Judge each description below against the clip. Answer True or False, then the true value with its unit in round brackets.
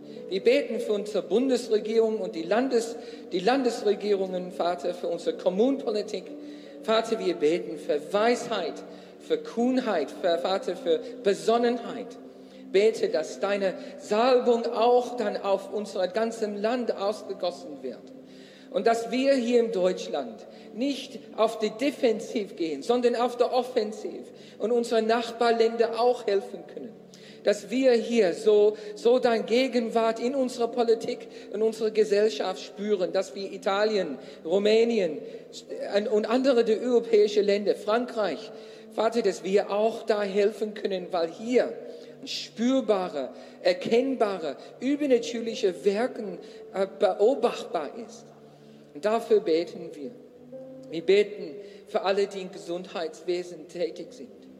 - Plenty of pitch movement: False (3.0 semitones)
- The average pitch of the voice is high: True (225 Hz)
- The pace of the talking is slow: True (120 wpm)